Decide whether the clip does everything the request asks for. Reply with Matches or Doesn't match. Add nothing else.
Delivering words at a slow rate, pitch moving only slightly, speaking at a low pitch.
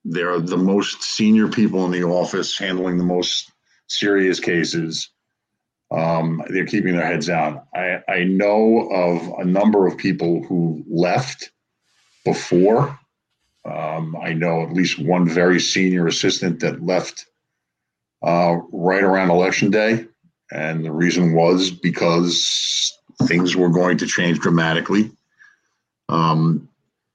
Matches